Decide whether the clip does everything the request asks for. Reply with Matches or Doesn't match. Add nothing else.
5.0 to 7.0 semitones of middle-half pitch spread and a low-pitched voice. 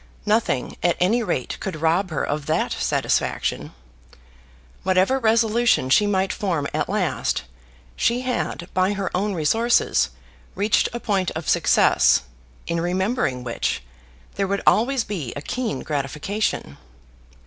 Doesn't match